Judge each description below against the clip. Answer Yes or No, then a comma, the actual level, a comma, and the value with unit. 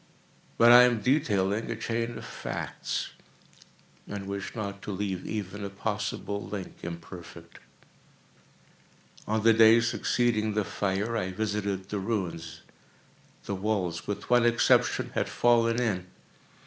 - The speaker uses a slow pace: Yes, slow, 125 wpm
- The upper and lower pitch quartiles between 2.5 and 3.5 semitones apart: Yes, average, 3.0 semitones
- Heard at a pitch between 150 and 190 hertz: No, low, 105 Hz